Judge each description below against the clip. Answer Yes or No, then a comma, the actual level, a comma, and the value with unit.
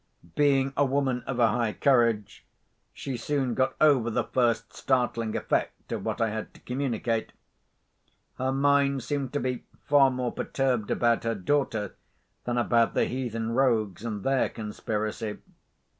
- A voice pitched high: No, low, 125 Hz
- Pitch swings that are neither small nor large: Yes, average, 3.0 semitones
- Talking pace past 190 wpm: No, average, 150 wpm